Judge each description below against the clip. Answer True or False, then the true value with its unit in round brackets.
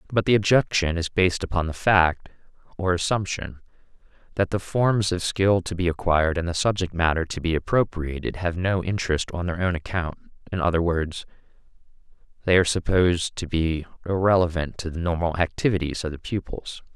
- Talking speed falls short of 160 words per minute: False (165 wpm)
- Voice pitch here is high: False (90 Hz)